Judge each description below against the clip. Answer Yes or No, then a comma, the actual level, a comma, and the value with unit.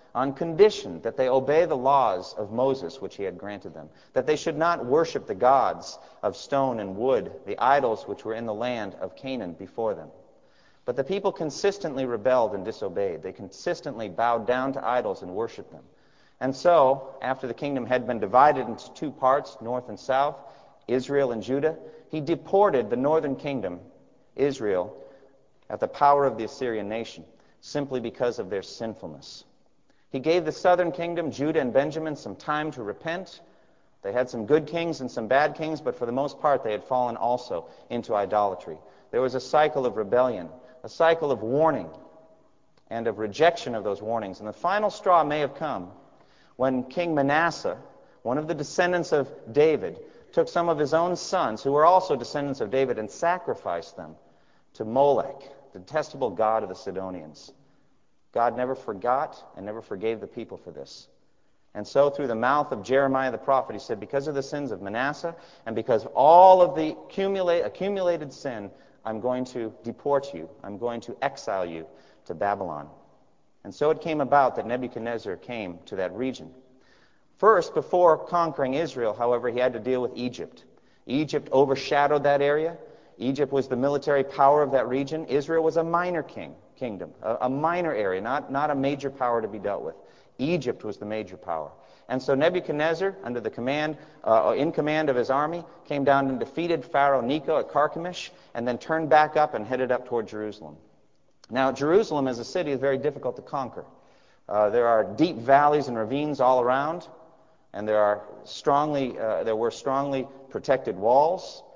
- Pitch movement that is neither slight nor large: Yes, average, 4.5 semitones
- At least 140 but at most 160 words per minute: No, average, 180 wpm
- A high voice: No, medium, 140 Hz